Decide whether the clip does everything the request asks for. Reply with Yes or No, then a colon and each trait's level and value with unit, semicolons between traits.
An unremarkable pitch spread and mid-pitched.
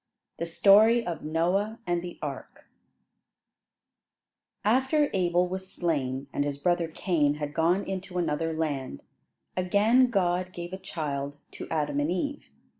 Yes: average, 4.0 semitones; medium, 175 Hz